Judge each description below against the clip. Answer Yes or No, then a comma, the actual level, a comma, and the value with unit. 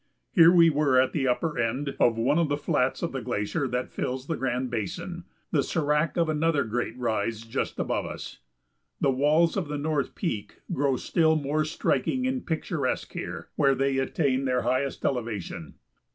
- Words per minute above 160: Yes, average, 180 wpm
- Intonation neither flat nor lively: Yes, average, 3.9 semitones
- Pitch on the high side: No, medium, 140 Hz